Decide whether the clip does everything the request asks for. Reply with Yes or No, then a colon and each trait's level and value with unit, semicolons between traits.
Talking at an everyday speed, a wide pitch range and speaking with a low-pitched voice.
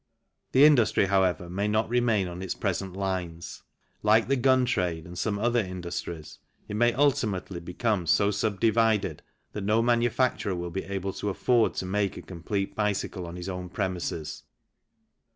No: average, 170 wpm; average, 3.8 semitones; low, 100 Hz